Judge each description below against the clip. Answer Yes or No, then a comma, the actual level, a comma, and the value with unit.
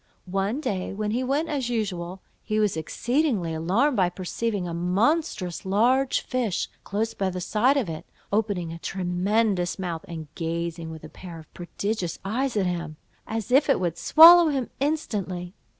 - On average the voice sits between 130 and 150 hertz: No, high, 195 Hz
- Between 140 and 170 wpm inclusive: Yes, average, 165 wpm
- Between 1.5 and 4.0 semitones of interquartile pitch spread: No, wide, 5.6 semitones